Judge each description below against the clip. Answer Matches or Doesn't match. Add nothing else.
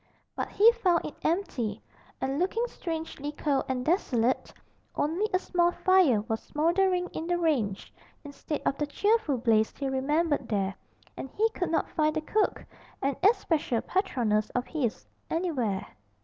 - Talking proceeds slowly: Doesn't match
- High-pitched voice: Matches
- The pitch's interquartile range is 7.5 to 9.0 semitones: Doesn't match